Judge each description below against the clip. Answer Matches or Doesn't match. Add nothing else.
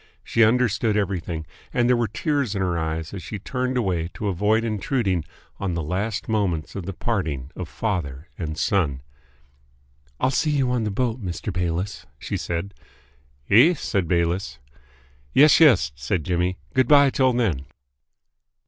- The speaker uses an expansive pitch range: Matches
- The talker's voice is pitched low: Matches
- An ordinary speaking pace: Matches